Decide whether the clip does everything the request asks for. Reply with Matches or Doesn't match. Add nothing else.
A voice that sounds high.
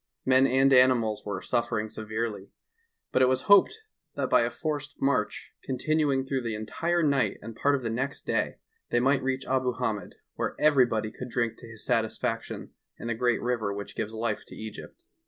Doesn't match